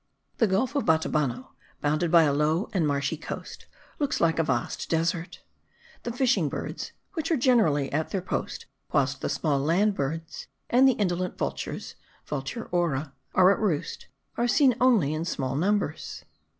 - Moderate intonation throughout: No, wide, 6.2 semitones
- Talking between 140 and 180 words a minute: Yes, average, 165 wpm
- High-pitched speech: No, medium, 165 Hz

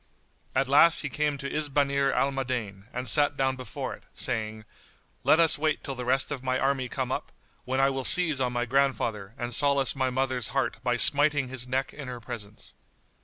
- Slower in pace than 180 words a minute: No, average, 200 wpm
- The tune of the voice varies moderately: No, narrow, 2.0 semitones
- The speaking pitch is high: No, low, 130 Hz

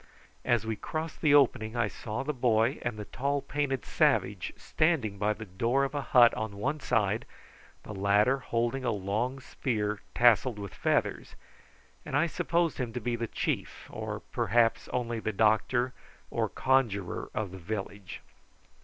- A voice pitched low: Yes, low, 115 Hz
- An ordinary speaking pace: Yes, average, 160 wpm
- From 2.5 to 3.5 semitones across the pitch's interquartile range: No, average, 4.0 semitones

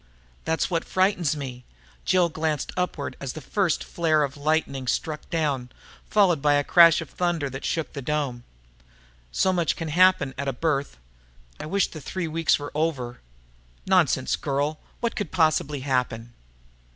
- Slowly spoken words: No, average, 160 wpm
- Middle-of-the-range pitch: Yes, medium, 155 Hz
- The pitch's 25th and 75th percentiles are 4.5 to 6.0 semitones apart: No, average, 3.3 semitones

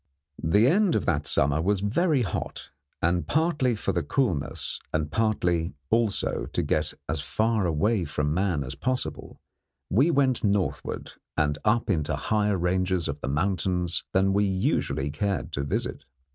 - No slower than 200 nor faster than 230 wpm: No, average, 155 wpm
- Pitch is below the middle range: Yes, very low, 95 Hz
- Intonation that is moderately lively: No, wide, 6.0 semitones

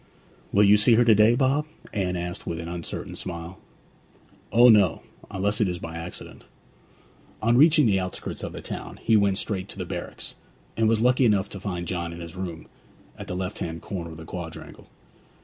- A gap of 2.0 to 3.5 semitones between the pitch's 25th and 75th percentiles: No, average, 4.1 semitones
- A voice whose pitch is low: Yes, very low, 95 Hz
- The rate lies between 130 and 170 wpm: No, average, 200 wpm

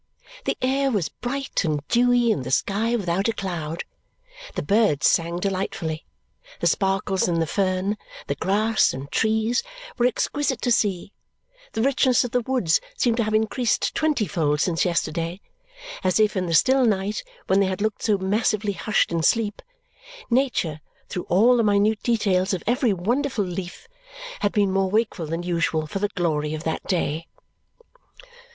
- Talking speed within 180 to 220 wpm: No, average, 165 wpm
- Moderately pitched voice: No, high, 200 Hz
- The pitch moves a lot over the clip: No, average, 4.8 semitones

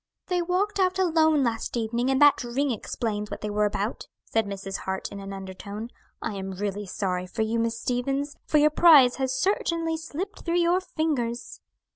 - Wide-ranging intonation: Yes, wide, 7.5 semitones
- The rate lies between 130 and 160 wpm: No, average, 185 wpm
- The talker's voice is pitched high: Yes, high, 245 Hz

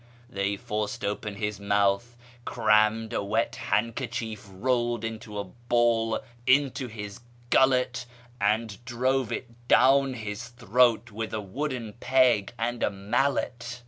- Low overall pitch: Yes, low, 115 Hz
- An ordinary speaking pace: No, slow, 125 wpm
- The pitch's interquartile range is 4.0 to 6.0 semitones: No, average, 2.8 semitones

